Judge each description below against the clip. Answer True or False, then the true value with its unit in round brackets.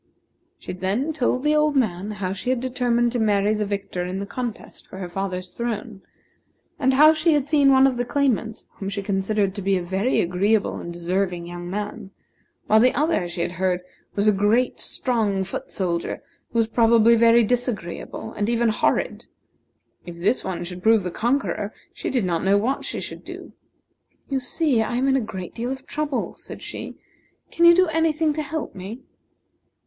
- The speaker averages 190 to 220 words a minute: True (195 wpm)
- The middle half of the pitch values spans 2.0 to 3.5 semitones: False (5.1 semitones)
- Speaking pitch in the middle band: False (220 Hz)